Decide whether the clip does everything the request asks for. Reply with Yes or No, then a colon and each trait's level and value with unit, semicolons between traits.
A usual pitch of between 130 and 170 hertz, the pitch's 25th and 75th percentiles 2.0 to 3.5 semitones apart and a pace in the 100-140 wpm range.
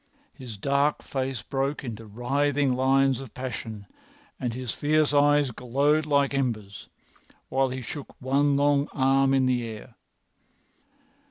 Yes: low, 135 Hz; narrow, 2.5 semitones; slow, 135 wpm